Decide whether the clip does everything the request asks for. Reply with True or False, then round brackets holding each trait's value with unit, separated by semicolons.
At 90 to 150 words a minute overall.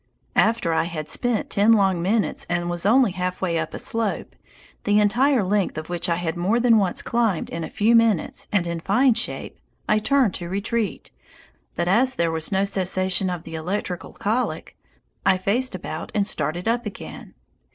False (185 wpm)